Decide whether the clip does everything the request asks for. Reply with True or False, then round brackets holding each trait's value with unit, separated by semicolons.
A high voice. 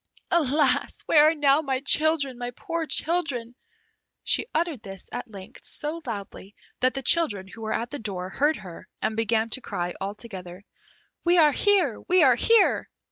True (255 Hz)